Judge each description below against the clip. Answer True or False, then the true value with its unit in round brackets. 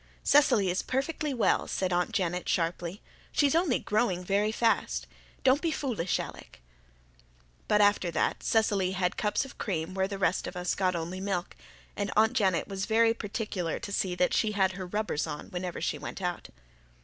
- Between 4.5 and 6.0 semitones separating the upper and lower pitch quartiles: False (3.7 semitones)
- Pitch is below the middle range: False (195 Hz)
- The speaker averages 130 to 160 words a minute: False (180 wpm)